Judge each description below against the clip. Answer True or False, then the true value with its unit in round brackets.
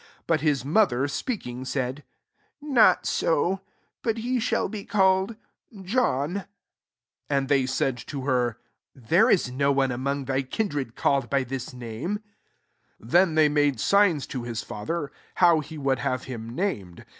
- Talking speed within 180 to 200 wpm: False (160 wpm)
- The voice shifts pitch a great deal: True (6.4 semitones)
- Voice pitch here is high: False (140 Hz)